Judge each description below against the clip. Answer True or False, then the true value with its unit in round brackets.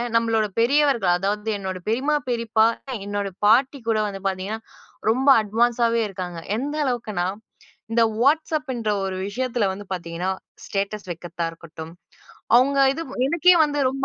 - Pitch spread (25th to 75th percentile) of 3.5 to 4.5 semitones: False (4.9 semitones)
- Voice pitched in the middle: False (220 Hz)